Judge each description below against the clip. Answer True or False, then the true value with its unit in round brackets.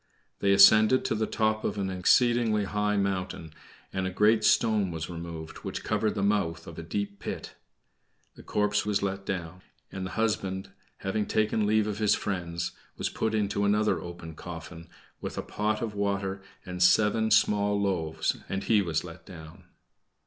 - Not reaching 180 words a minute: True (170 wpm)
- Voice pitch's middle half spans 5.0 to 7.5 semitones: False (3.0 semitones)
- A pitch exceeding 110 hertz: False (100 Hz)